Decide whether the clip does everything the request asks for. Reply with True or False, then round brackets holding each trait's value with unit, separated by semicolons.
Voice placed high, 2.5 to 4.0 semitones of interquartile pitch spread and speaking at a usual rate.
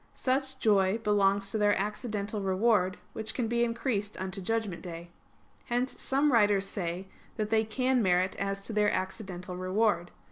True (205 Hz; 3.2 semitones; 155 wpm)